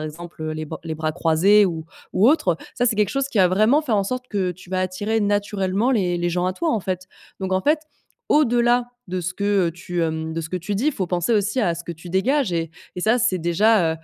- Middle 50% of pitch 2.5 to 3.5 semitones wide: No, average, 4.2 semitones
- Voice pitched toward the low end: No, medium, 185 Hz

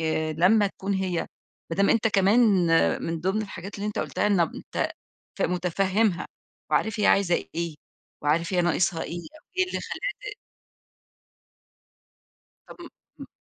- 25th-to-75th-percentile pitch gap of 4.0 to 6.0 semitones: No, average, 3.6 semitones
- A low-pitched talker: No, high, 190 Hz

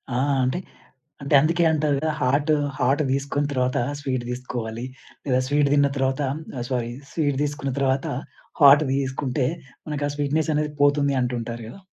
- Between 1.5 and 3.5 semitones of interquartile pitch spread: Yes, narrow, 2.4 semitones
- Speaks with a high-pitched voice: No, medium, 140 Hz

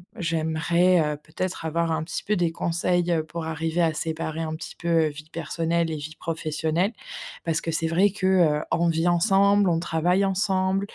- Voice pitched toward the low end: No, medium, 165 Hz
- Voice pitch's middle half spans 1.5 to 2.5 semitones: Yes, narrow, 1.9 semitones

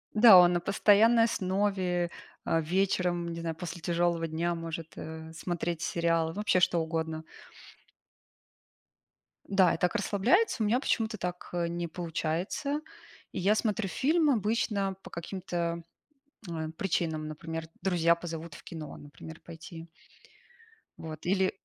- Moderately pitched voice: Yes, medium, 175 Hz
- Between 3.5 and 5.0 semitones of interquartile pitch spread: No, average, 3.1 semitones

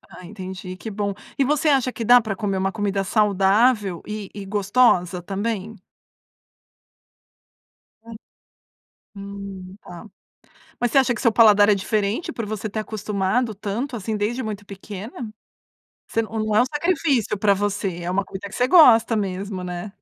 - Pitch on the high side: Yes, high, 210 Hz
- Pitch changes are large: No, average, 2.8 semitones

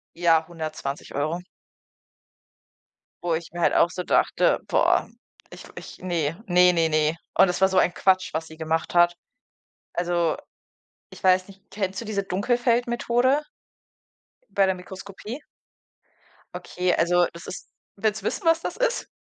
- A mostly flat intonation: No, average, 3.0 semitones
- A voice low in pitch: No, medium, 180 Hz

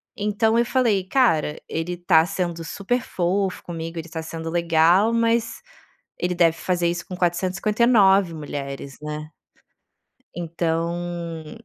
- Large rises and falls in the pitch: No, average, 3.5 semitones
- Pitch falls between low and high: Yes, medium, 175 Hz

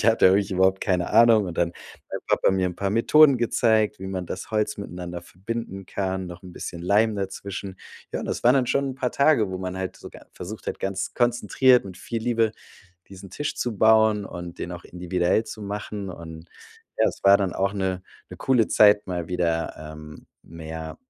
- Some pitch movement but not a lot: Yes, average, 3.6 semitones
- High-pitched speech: No, very low, 95 Hz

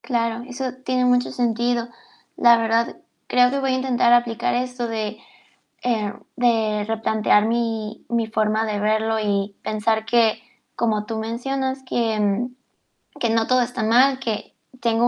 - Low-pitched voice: No, high, 230 Hz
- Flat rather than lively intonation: Yes, narrow, 2.0 semitones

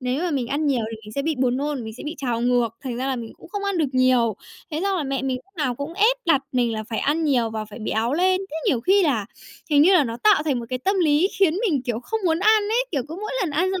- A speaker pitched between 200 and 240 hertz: No, very high, 280 Hz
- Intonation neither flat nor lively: No, wide, 6.2 semitones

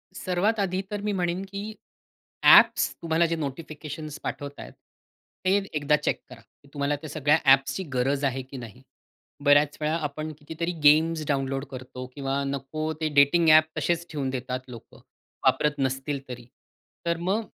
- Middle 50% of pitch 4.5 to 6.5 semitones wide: No, average, 3.6 semitones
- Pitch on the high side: No, medium, 150 Hz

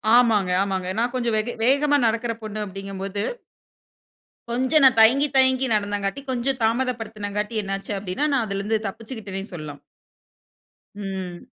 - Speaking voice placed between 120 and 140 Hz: No, high, 215 Hz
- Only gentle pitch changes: No, average, 3.9 semitones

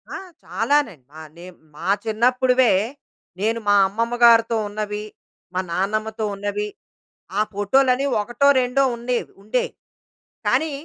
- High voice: Yes, high, 225 Hz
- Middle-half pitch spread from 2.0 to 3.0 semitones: No, average, 3.4 semitones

